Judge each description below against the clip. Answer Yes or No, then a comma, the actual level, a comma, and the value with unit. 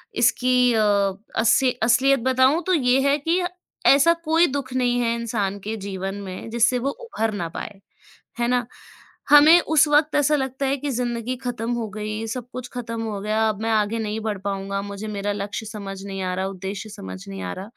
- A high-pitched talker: Yes, high, 230 Hz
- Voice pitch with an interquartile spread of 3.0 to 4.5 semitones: Yes, average, 4.2 semitones